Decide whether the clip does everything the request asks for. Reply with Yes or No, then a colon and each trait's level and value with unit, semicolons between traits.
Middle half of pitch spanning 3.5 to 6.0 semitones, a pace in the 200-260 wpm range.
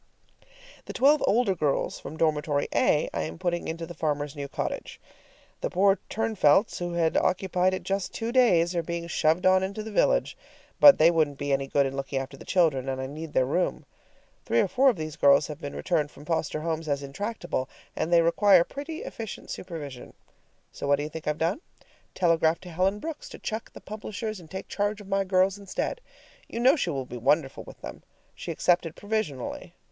Yes: average, 5.1 semitones; fast, 205 wpm